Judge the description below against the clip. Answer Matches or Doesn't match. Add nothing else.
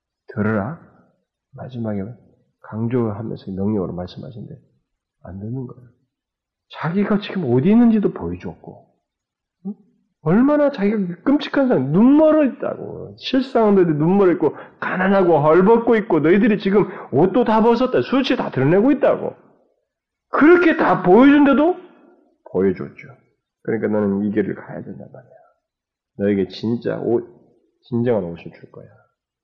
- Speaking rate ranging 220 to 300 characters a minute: Matches